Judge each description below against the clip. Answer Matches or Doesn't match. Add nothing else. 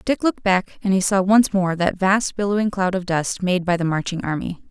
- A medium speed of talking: Doesn't match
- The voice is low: Doesn't match